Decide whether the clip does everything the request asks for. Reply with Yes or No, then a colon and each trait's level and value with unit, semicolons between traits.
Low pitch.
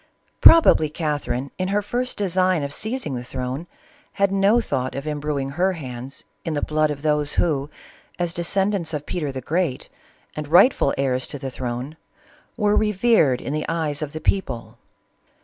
No: medium, 155 Hz